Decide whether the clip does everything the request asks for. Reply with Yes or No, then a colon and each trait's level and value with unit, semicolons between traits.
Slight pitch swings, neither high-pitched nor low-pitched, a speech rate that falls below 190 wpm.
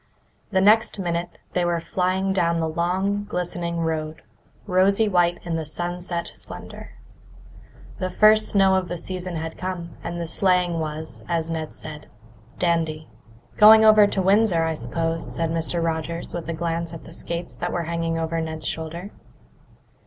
Yes: narrow, 2.1 semitones; medium, 170 Hz; average, 160 wpm